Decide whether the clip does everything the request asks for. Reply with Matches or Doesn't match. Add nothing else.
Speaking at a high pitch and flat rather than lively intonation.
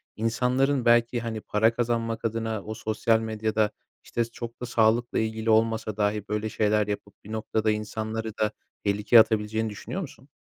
Doesn't match